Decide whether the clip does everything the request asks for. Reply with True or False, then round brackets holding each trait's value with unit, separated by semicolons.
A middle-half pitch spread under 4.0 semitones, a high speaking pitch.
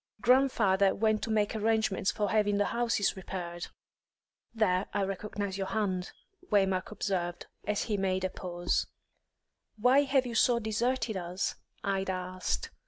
True (2.8 semitones; 205 Hz)